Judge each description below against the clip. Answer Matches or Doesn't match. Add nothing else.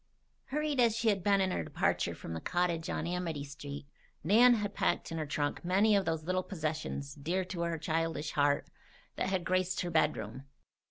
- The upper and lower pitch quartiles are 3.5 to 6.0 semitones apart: Matches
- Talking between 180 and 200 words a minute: Matches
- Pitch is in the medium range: Matches